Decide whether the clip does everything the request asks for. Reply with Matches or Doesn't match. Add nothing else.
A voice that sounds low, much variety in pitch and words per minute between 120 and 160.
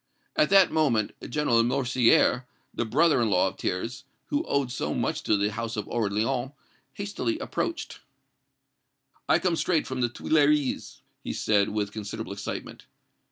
Matches